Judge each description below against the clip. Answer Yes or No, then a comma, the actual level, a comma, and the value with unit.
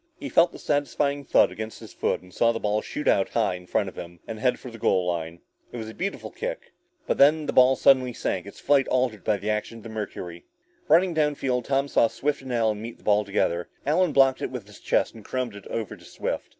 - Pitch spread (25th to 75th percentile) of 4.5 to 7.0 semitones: Yes, average, 5.1 semitones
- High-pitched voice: No, low, 115 Hz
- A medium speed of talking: No, fast, 250 wpm